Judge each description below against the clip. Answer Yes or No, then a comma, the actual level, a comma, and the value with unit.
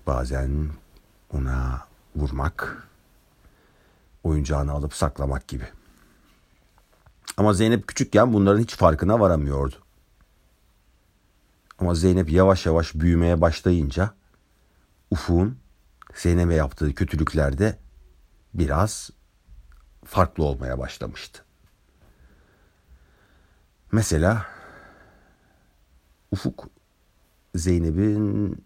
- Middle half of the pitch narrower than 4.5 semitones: No, average, 5.2 semitones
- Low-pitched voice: Yes, very low, 80 Hz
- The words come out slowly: Yes, slow, 65 wpm